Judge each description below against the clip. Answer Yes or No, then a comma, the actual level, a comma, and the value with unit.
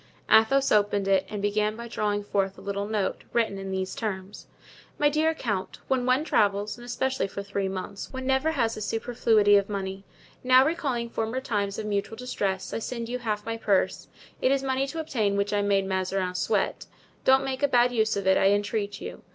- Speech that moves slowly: No, average, 200 wpm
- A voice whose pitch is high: Yes, high, 215 Hz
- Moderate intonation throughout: Yes, average, 4.0 semitones